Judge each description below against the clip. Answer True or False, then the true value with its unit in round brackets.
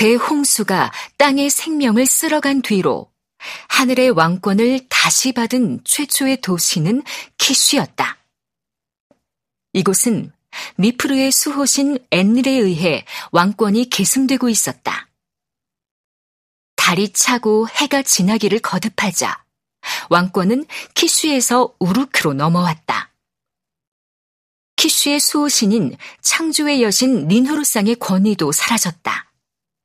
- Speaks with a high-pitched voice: True (235 Hz)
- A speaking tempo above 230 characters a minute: False (225 characters per minute)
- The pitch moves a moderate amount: False (5.9 semitones)